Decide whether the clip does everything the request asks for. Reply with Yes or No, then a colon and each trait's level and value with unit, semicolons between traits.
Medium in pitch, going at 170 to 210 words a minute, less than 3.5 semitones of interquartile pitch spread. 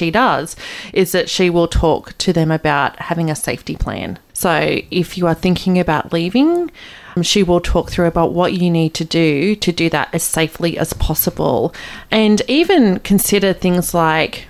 Yes: medium, 175 Hz; average, 175 wpm; narrow, 2.6 semitones